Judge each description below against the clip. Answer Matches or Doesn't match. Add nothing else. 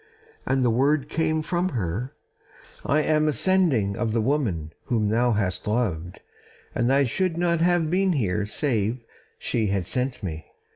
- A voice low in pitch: Matches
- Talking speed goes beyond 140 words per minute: Matches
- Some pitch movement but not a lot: Doesn't match